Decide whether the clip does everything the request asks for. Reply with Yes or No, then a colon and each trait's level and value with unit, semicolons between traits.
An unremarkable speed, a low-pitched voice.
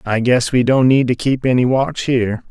No: fast, 240 wpm; low, 125 Hz